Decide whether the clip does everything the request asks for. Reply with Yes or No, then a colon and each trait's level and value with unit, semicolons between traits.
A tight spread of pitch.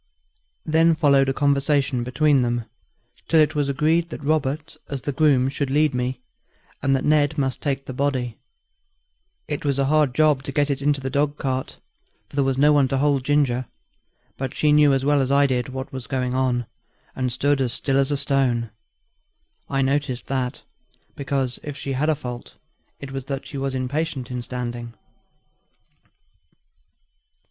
Yes: narrow, 2.1 semitones